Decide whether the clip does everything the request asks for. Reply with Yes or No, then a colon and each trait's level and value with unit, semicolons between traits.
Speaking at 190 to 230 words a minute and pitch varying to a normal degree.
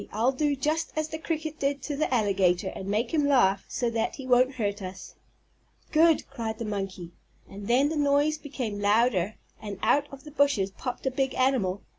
No: average, 195 wpm; wide, 5.9 semitones